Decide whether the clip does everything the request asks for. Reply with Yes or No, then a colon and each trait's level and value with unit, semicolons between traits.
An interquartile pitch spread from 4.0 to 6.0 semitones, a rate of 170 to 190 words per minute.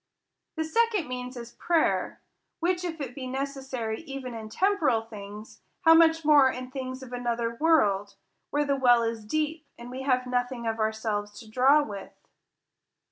Yes: average, 4.6 semitones; average, 175 wpm